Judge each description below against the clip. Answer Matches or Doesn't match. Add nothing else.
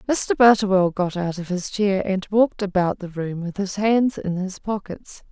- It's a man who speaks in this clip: Doesn't match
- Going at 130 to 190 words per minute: Doesn't match